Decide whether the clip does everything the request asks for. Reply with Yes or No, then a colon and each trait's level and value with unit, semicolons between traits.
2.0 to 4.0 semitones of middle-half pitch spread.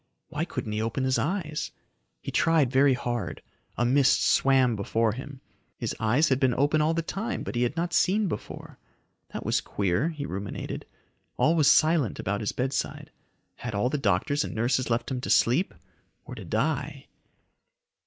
No: average, 4.7 semitones